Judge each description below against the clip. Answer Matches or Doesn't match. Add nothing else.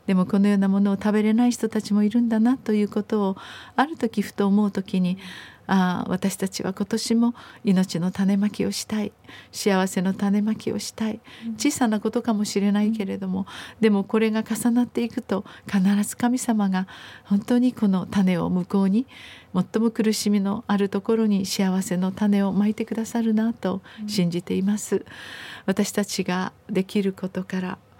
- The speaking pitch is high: Matches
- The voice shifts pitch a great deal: Doesn't match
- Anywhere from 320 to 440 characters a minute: Matches